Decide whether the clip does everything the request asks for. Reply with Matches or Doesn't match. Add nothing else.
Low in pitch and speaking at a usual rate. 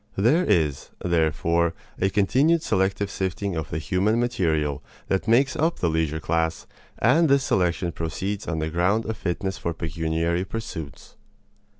Matches